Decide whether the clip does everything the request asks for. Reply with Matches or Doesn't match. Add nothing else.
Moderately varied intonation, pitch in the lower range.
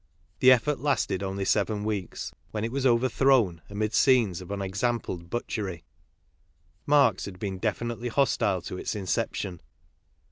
Matches